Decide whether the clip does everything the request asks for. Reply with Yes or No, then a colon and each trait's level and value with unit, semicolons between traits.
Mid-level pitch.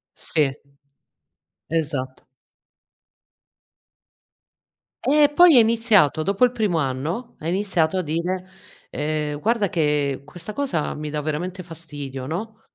Yes: medium, 165 Hz